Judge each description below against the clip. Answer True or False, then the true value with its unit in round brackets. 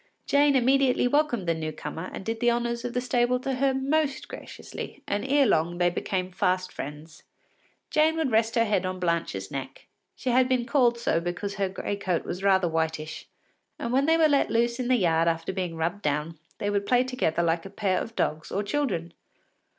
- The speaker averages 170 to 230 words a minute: True (205 wpm)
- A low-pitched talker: False (205 Hz)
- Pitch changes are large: True (6.8 semitones)